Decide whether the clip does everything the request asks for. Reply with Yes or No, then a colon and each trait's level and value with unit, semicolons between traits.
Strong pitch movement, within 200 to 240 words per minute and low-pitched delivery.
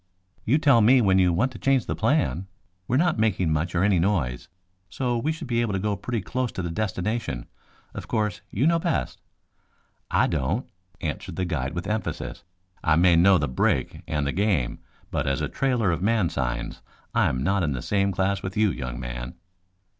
Yes: wide, 6.1 semitones; fast, 205 wpm; very low, 95 Hz